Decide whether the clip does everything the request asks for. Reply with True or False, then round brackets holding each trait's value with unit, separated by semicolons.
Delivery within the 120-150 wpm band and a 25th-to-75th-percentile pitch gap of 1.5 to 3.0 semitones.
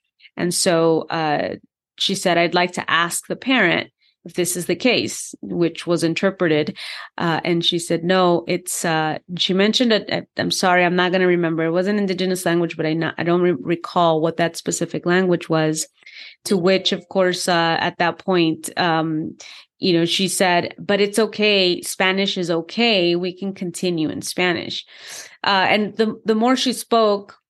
False (185 wpm; 2.4 semitones)